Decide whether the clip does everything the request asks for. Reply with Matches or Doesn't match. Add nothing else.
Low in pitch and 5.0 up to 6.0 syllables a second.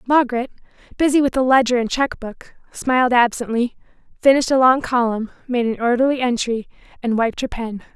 Doesn't match